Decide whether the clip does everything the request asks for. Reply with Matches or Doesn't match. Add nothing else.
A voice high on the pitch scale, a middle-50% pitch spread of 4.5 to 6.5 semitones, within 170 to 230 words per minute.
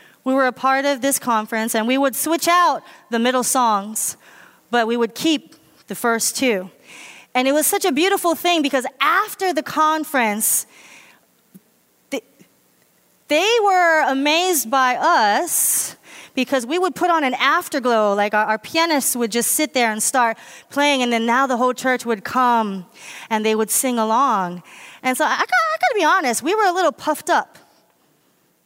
Matches